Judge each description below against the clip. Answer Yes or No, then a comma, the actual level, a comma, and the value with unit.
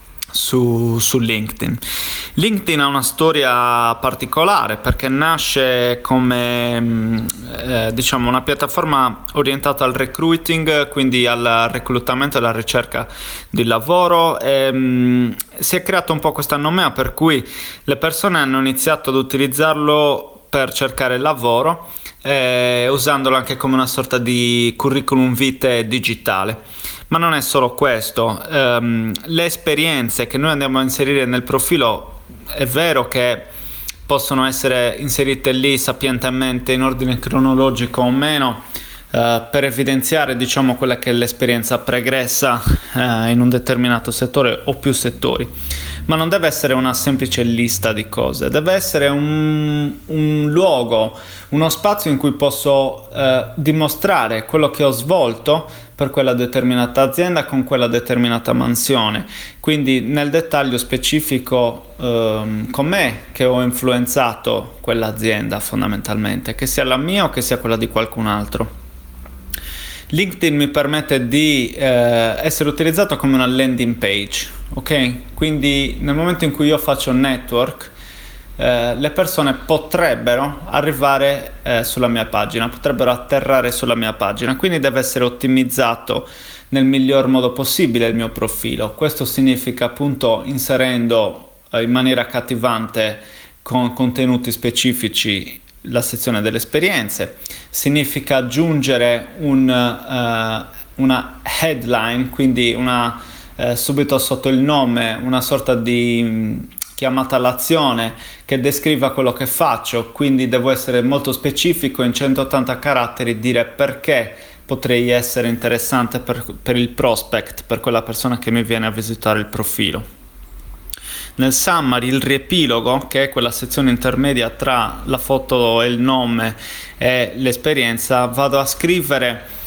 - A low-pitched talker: Yes, low, 130 Hz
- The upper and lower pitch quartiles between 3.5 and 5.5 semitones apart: No, average, 2.7 semitones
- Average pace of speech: Yes, average, 135 wpm